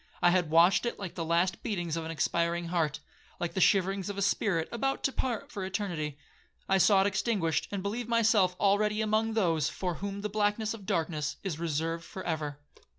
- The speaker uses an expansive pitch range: No, average, 3.7 semitones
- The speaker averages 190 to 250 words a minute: Yes, average, 200 wpm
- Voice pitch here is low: No, high, 190 Hz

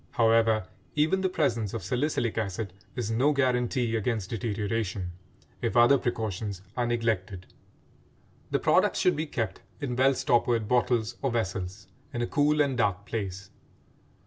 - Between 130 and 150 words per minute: Yes, average, 145 wpm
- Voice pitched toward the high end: No, low, 115 Hz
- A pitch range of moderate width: Yes, average, 3.5 semitones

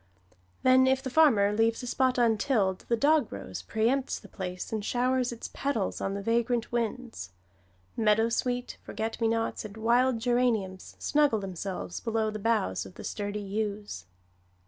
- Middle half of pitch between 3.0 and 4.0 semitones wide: Yes, average, 3.4 semitones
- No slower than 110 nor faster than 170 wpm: Yes, average, 155 wpm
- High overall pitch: Yes, high, 225 Hz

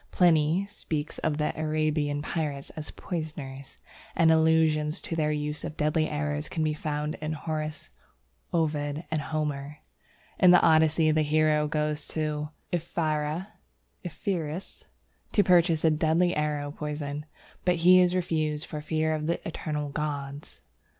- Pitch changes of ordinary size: No, narrow, 1.3 semitones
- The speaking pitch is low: No, medium, 155 Hz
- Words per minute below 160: Yes, average, 140 wpm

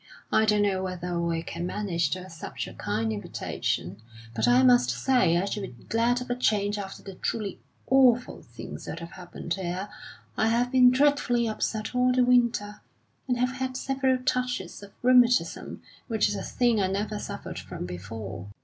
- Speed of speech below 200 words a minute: Yes, average, 180 wpm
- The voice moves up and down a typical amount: No, wide, 6.4 semitones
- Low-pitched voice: No, high, 205 Hz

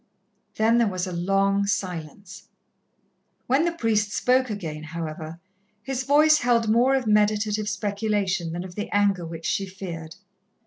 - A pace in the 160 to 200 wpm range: No, average, 145 wpm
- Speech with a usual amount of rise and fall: Yes, average, 4.3 semitones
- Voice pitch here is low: No, high, 205 Hz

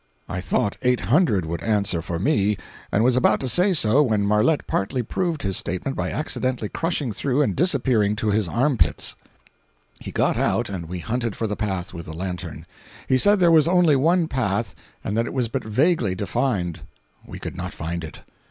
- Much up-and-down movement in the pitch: Yes, wide, 6.4 semitones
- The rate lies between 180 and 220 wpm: Yes, fast, 205 wpm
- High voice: No, low, 110 Hz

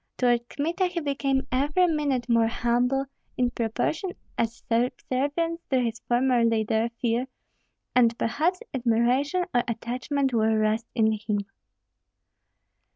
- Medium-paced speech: No, slow, 120 wpm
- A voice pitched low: No, high, 245 Hz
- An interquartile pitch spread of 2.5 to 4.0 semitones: Yes, average, 3.5 semitones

